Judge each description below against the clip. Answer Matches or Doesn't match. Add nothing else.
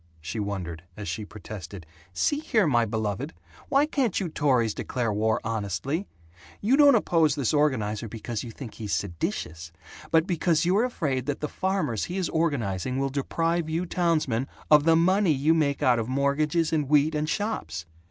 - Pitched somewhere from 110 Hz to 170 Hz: Matches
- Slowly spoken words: Doesn't match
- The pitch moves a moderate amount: Doesn't match